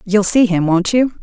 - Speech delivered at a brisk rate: Yes, fast, 245 wpm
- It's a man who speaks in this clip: No, female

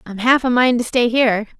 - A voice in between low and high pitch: No, high, 240 Hz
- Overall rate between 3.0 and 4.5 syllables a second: No, 5.8 syllables/s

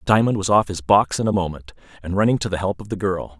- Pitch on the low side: Yes, very low, 95 Hz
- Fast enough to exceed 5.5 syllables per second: Yes, 6.3 syllables/s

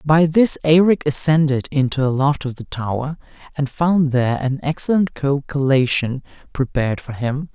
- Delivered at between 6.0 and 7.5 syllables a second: No, 4.8 syllables/s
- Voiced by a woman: No, male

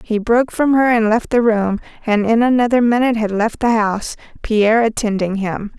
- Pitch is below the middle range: No, high, 225 Hz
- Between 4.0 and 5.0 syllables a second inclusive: No, 5.4 syllables/s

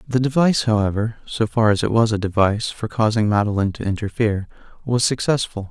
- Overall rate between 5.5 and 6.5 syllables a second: Yes, 6.2 syllables/s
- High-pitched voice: No, low, 110 Hz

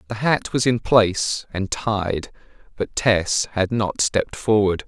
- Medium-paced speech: Yes, average, 160 wpm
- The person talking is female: No, male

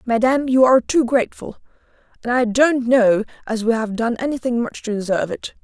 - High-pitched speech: Yes, high, 240 Hz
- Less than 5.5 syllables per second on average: No, 5.9 syllables/s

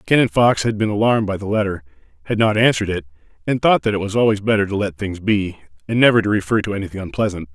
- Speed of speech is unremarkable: No, fast, 240 wpm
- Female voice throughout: No, male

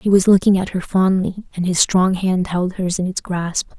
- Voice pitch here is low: No, medium, 185 Hz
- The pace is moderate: No, fast, 240 wpm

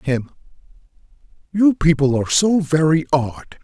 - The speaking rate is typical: No, slow, 115 wpm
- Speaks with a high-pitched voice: No, medium, 155 Hz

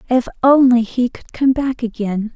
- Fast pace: No, average, 180 wpm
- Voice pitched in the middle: No, high, 245 Hz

